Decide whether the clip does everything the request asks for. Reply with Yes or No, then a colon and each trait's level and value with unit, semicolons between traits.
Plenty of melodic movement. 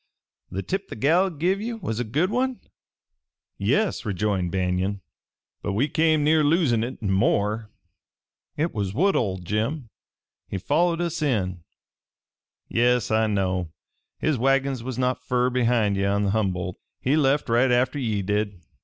Yes: wide, 6.8 semitones